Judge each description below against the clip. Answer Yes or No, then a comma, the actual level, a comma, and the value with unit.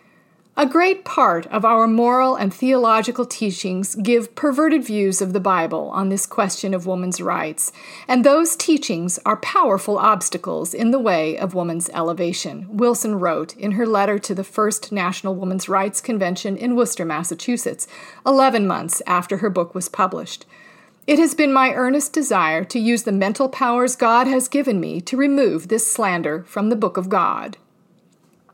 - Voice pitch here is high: Yes, high, 215 Hz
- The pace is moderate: Yes, average, 165 wpm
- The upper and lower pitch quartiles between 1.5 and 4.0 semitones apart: No, average, 5.1 semitones